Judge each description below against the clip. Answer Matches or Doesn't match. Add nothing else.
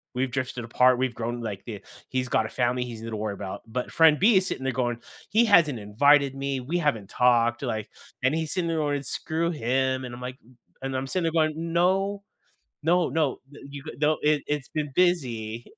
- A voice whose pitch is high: Doesn't match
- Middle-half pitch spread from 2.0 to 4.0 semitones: Doesn't match